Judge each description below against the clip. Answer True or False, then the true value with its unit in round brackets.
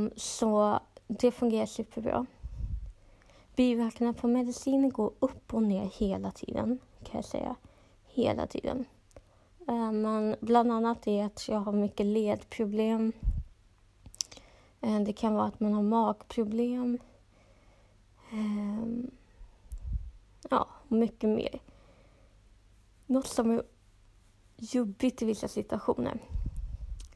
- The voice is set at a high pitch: True (215 Hz)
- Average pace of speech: False (95 wpm)